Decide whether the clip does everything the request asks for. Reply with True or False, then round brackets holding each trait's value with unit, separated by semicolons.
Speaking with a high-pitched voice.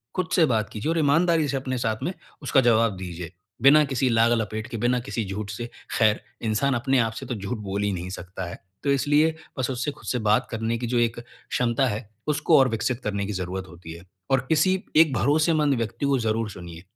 False (120 Hz)